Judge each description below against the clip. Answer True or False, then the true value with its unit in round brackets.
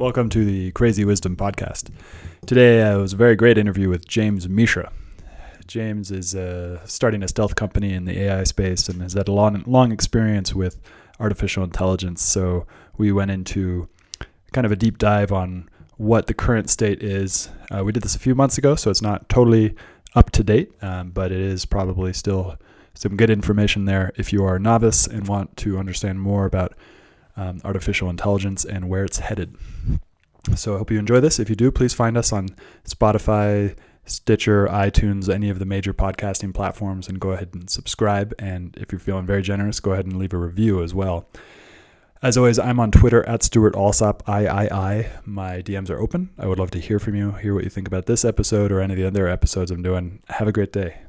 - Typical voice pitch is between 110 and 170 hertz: False (100 Hz)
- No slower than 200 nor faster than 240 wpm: True (205 wpm)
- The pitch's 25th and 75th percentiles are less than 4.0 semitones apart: True (2.4 semitones)